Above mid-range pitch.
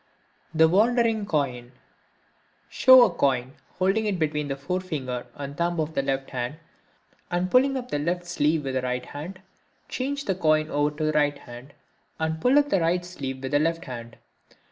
No: medium, 155 Hz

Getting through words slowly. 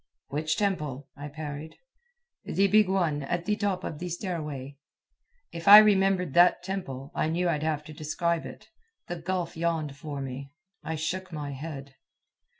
No: average, 160 wpm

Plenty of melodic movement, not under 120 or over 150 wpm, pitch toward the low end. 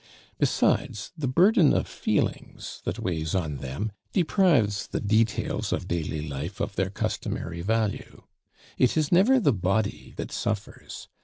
Yes: wide, 8.5 semitones; average, 140 wpm; low, 105 Hz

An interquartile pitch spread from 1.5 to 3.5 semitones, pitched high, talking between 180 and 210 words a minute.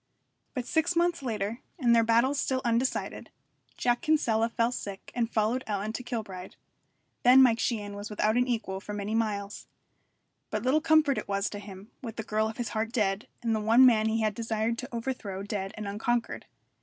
Yes: average, 2.9 semitones; high, 225 Hz; average, 195 wpm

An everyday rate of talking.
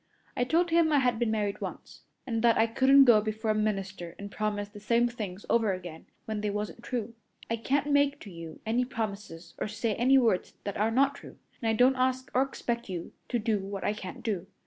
No: fast, 225 wpm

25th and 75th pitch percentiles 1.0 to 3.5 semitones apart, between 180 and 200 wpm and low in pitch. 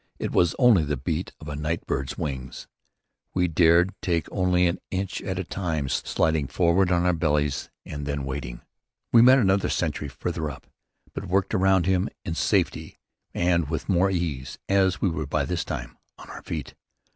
No: average, 3.9 semitones; average, 185 wpm; very low, 85 Hz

